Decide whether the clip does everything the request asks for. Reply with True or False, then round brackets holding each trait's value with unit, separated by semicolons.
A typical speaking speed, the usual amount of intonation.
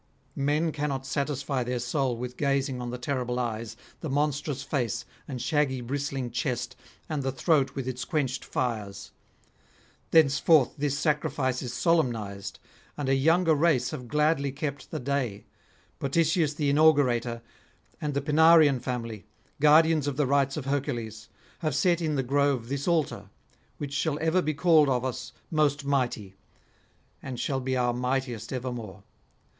True (150 wpm; 3.2 semitones)